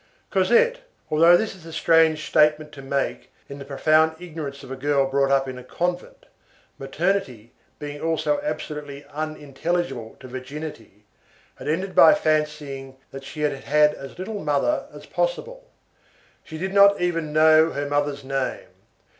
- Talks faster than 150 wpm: No, average, 145 wpm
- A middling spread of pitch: Yes, average, 3.5 semitones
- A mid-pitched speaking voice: Yes, medium, 150 Hz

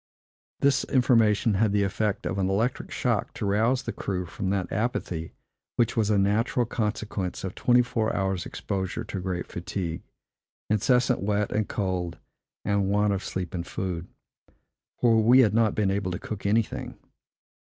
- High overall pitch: No, low, 100 Hz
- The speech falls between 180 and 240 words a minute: No, average, 165 wpm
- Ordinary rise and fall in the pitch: Yes, average, 3.0 semitones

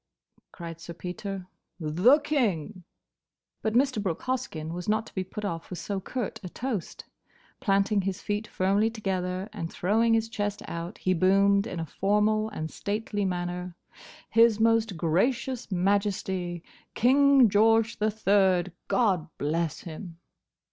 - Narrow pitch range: No, average, 3.6 semitones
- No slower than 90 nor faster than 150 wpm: Yes, average, 140 wpm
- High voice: Yes, high, 200 Hz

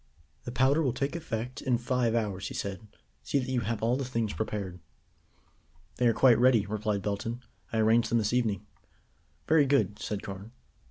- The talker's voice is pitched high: No, low, 115 Hz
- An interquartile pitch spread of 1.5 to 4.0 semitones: Yes, average, 3.1 semitones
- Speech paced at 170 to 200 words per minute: Yes, average, 180 wpm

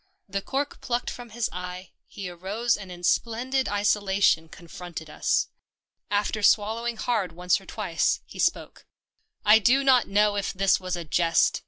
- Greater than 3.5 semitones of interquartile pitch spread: Yes, average, 4.3 semitones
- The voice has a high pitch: Yes, high, 205 Hz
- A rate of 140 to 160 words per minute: No, average, 170 wpm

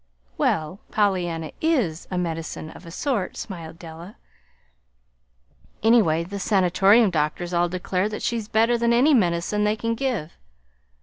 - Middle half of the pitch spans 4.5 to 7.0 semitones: Yes, average, 4.9 semitones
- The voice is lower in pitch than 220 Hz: Yes, high, 190 Hz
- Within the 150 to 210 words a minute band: No, slow, 135 wpm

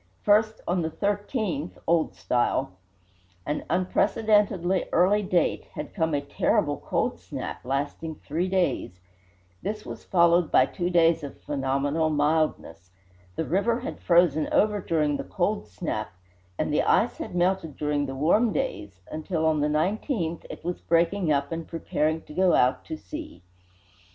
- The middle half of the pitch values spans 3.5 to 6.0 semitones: Yes, average, 4.2 semitones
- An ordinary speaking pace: Yes, average, 150 wpm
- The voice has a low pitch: No, medium, 165 Hz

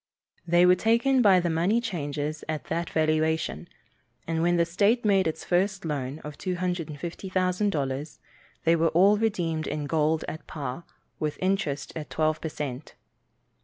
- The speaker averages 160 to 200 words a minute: No, average, 150 wpm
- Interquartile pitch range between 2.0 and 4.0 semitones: Yes, average, 3.3 semitones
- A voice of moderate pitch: Yes, medium, 165 Hz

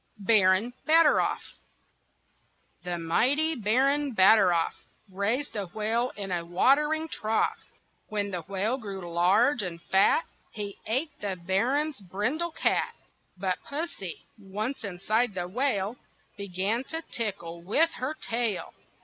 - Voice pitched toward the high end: Yes, high, 210 Hz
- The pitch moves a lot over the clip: Yes, wide, 5.8 semitones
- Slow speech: Yes, slow, 120 wpm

